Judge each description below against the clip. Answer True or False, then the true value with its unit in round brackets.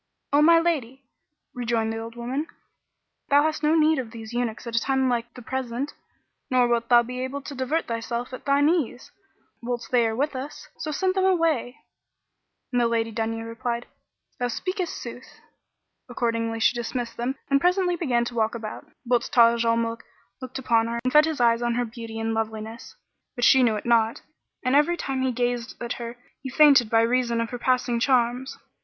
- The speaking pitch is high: True (245 Hz)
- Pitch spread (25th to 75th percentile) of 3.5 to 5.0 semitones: False (2.7 semitones)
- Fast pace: False (195 wpm)